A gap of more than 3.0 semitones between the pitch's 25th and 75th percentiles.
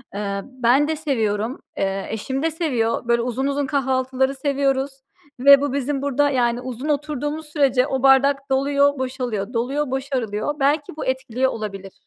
No: average, 2.7 semitones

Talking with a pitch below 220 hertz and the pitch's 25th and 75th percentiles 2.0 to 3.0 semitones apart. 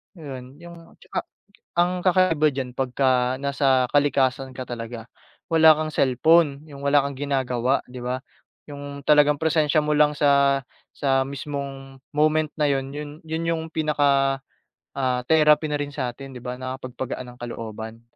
Yes: medium, 140 Hz; narrow, 2.6 semitones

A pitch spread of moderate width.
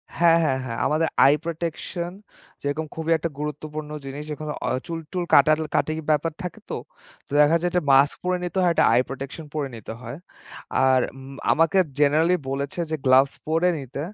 Yes: average, 3.0 semitones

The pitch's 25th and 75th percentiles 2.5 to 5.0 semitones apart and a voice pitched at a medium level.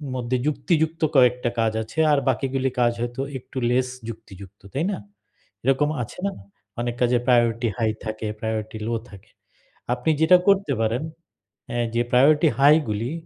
No: average, 3.4 semitones; low, 125 Hz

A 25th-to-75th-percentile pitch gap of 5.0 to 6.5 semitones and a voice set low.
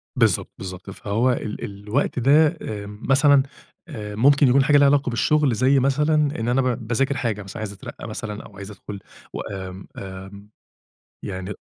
Yes: average, 5.3 semitones; low, 115 Hz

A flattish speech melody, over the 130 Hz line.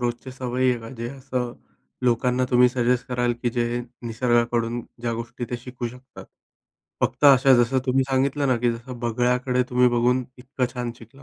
No: narrow, 1.2 semitones; low, 125 Hz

